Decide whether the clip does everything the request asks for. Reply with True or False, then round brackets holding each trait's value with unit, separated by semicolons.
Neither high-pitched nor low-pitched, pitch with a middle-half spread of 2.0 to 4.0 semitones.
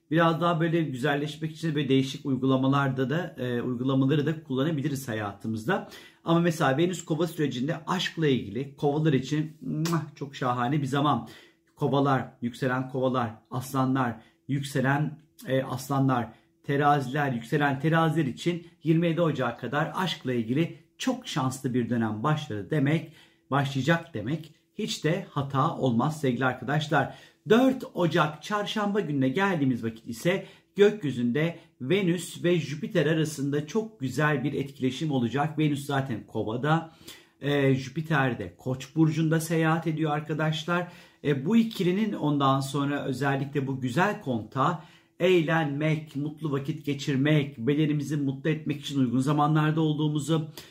True (150 Hz; 3.7 semitones)